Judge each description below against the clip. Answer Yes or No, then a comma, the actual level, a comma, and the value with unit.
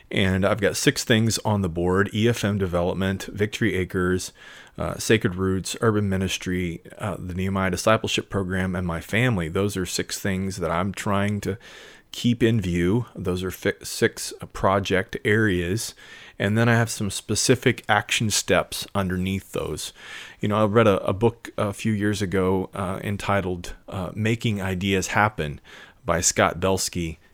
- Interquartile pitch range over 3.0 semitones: No, narrow, 2.6 semitones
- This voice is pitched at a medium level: No, low, 100 Hz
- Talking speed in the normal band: Yes, average, 160 wpm